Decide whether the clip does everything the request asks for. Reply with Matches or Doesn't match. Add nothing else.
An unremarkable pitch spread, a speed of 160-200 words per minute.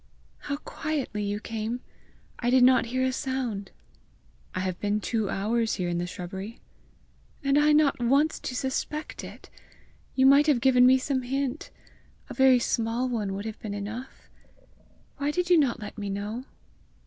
Matches